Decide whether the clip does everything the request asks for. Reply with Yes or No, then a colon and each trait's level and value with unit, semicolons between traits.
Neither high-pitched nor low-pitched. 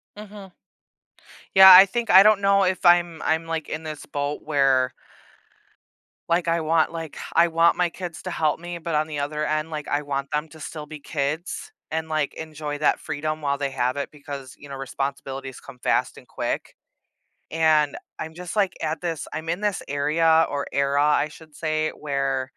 Yes: medium, 155 Hz